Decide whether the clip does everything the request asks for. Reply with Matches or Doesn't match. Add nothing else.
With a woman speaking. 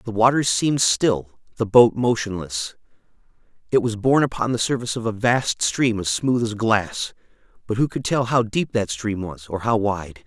Doesn't match